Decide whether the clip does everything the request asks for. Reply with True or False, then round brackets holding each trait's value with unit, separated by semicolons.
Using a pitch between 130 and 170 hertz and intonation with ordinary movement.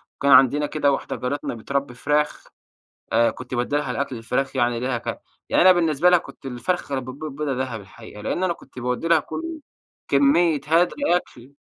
True (140 Hz; 3.7 semitones)